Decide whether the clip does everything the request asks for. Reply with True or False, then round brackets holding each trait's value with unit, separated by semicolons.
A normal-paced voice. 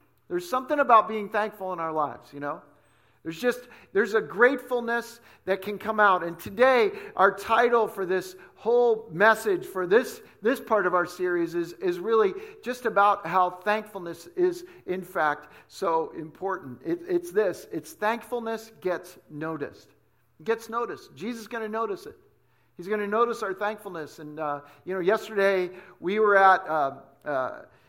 True (170 wpm)